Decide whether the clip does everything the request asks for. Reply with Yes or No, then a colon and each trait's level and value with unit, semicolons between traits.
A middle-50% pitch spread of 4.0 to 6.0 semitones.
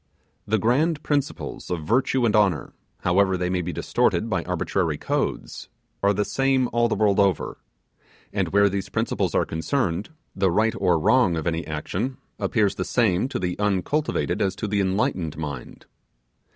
Yes: average, 4.4 semitones